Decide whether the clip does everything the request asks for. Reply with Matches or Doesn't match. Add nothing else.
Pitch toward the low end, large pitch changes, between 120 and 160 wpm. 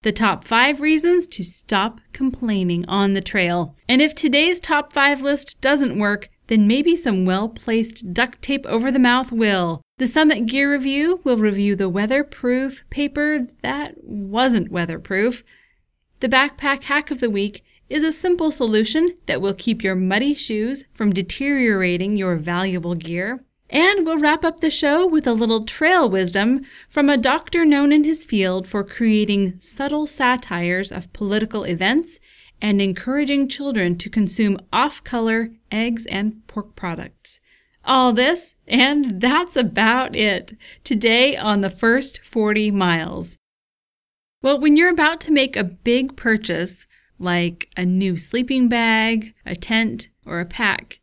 Doesn't match